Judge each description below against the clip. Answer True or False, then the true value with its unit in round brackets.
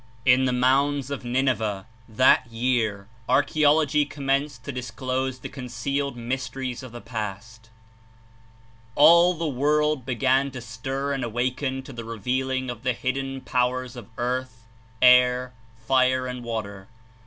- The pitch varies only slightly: True (2.0 semitones)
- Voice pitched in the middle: False (130 Hz)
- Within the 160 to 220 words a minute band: False (135 wpm)